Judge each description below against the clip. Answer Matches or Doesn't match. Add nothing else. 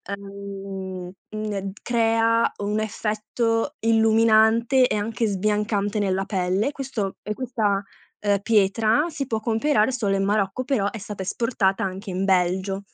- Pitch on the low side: Doesn't match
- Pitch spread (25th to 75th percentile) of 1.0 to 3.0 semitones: Matches